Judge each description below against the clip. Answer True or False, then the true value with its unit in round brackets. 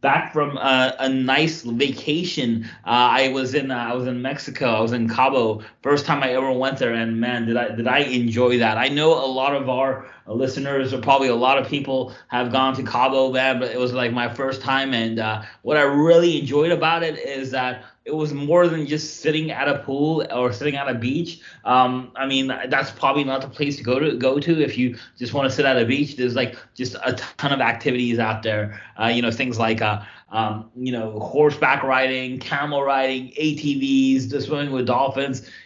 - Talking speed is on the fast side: True (220 wpm)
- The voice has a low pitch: True (130 Hz)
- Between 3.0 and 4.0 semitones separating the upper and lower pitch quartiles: False (2.4 semitones)